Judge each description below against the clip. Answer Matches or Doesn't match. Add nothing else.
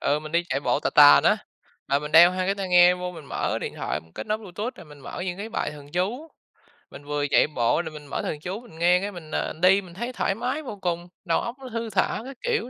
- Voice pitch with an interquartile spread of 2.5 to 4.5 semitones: Doesn't match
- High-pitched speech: Doesn't match